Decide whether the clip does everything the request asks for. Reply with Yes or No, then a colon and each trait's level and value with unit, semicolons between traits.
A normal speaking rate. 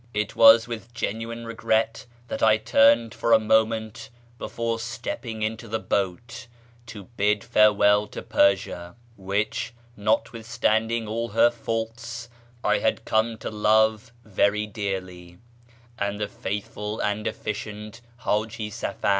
No: slow, 125 wpm